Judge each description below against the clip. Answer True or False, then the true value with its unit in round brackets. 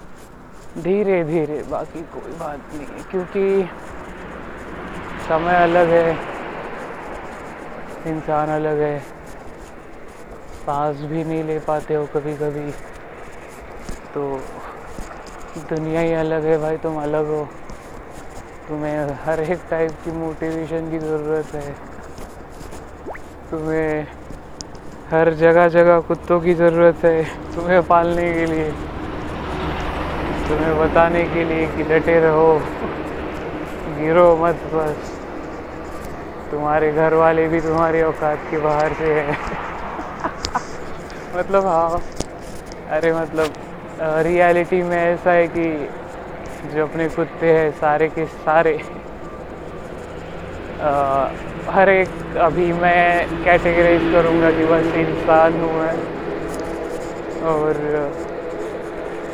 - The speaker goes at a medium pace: True (100 wpm)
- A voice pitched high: False (160 Hz)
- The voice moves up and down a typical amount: False (1.8 semitones)